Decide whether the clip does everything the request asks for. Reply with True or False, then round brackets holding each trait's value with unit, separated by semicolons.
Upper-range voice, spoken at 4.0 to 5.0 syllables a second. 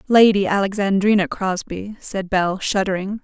True (195 Hz; 4.6 syllables/s)